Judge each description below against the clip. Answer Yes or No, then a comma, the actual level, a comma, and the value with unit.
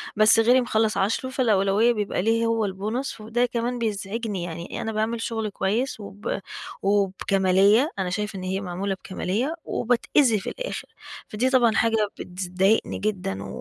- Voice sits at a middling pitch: No, high, 215 Hz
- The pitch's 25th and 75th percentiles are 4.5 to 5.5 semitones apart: No, average, 3.1 semitones